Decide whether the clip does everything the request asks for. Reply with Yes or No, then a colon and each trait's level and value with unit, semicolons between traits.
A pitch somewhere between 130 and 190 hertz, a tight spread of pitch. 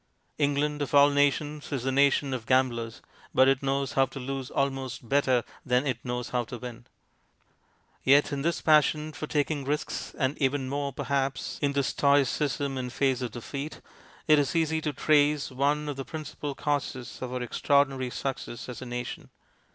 Yes: medium, 140 Hz; narrow, 1.9 semitones